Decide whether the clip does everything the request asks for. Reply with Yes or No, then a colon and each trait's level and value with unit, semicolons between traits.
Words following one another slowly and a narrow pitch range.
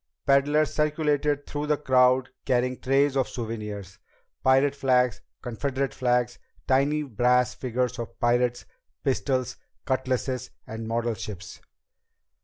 Yes: slow, 110 wpm; narrow, 2.3 semitones